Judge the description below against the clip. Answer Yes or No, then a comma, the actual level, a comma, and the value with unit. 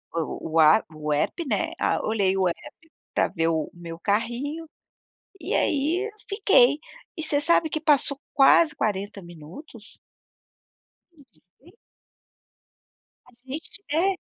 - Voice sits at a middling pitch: No, very high, 250 Hz